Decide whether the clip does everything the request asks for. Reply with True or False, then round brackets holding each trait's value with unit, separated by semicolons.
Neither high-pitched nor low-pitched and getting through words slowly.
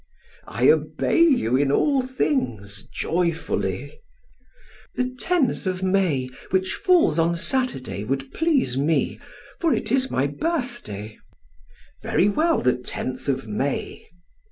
True (180 Hz; 120 wpm)